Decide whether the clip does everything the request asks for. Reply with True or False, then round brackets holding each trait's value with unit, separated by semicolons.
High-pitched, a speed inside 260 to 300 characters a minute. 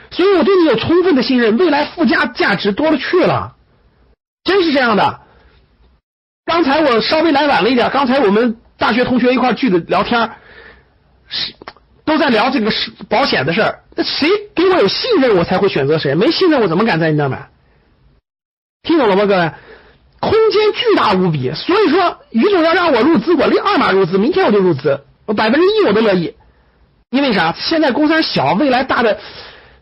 True (275 Hz; 280 characters per minute)